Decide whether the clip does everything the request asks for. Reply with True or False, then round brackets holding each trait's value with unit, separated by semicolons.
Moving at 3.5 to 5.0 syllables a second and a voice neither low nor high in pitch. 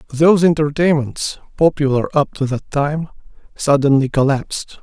True (4.9 syllables/s; 145 Hz)